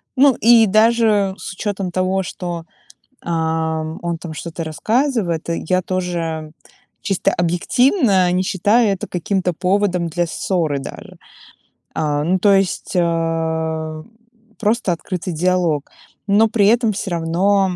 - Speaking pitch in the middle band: Yes, medium, 180 Hz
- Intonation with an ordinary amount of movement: Yes, average, 3.6 semitones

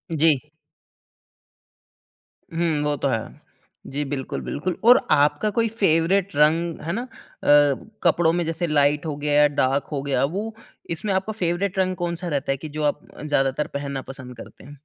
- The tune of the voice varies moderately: Yes, average, 3.4 semitones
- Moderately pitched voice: Yes, medium, 155 Hz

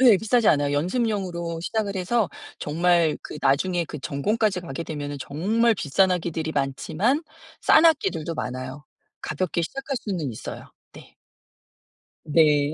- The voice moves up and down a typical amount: No, wide, 6.3 semitones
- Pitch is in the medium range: Yes, medium, 170 Hz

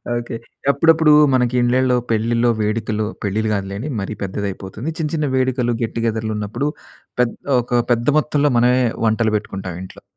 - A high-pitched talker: No, low, 115 Hz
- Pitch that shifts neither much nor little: Yes, average, 3.2 semitones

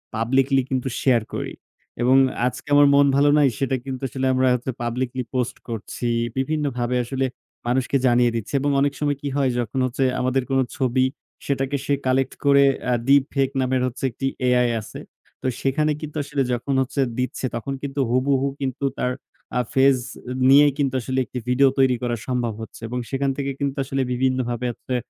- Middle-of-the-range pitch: No, low, 130 Hz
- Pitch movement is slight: Yes, narrow, 1.8 semitones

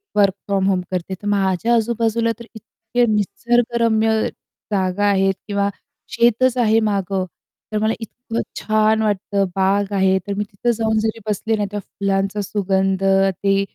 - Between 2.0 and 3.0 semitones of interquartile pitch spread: Yes, narrow, 2.4 semitones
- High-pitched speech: Yes, high, 205 Hz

